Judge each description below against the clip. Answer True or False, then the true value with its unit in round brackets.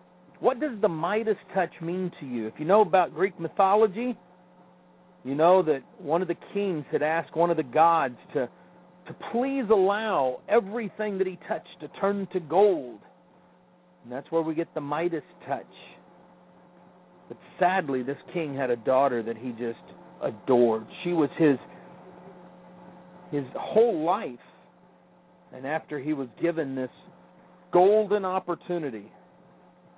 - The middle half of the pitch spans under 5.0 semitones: True (4.0 semitones)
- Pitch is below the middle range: False (175 Hz)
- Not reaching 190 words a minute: True (145 wpm)